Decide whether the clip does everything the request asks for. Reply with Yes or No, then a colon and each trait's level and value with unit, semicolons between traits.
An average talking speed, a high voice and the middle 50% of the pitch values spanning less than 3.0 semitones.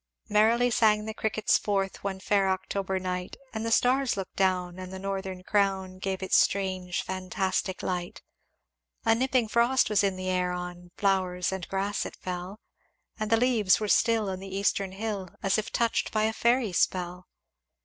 Yes: average, 175 wpm; high, 195 Hz; narrow, 2.6 semitones